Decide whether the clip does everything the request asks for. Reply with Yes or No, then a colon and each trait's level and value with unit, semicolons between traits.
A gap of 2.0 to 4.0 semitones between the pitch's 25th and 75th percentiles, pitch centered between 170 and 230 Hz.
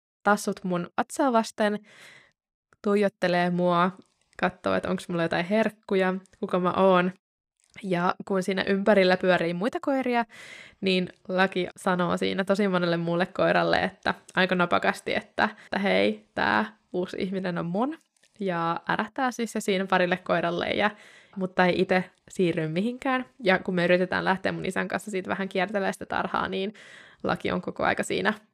Yes: narrow, 2.6 semitones; high, 190 Hz